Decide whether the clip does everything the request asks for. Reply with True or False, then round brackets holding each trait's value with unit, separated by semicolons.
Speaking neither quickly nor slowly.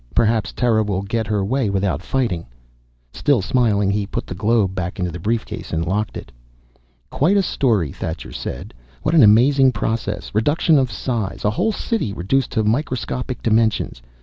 True (170 wpm)